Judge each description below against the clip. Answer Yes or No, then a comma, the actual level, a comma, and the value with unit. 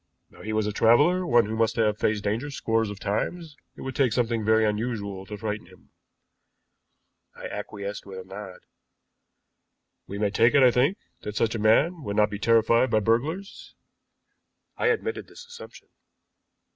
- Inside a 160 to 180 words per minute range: Yes, average, 170 wpm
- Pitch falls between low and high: No, low, 110 Hz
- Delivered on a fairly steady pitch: No, average, 3.6 semitones